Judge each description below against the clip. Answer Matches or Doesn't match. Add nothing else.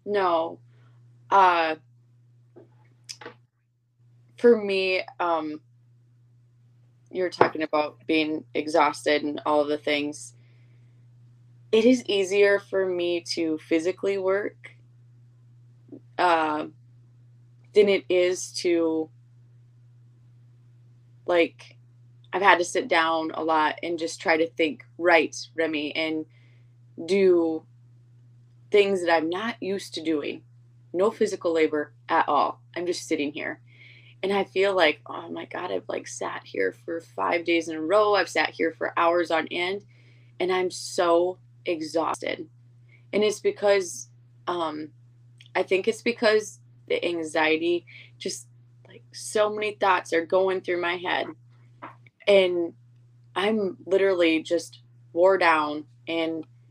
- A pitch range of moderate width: Doesn't match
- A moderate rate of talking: Doesn't match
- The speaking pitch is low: Doesn't match